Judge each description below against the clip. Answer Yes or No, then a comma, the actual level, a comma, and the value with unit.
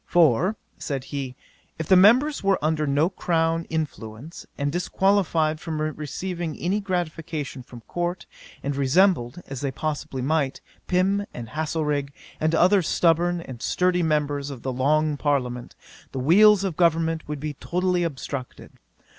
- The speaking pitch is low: No, medium, 160 Hz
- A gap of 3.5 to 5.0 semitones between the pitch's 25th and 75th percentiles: Yes, average, 3.9 semitones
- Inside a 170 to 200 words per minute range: No, average, 145 wpm